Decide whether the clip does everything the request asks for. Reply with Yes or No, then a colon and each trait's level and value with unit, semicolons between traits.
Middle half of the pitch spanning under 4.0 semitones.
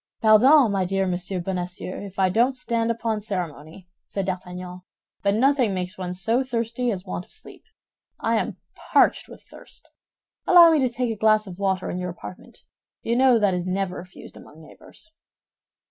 No: average, 4.3 semitones